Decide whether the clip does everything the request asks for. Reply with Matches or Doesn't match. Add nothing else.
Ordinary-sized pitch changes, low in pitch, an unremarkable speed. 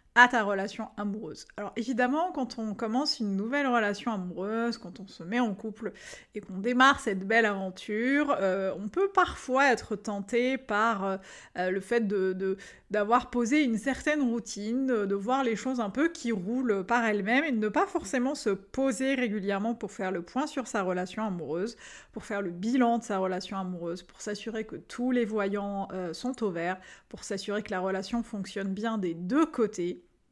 Doesn't match